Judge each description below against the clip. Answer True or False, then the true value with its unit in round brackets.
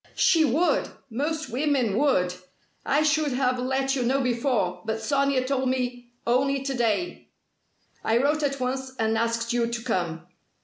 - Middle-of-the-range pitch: False (255 Hz)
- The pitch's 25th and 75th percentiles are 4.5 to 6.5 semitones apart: False (3.1 semitones)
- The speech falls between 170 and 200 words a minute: False (160 wpm)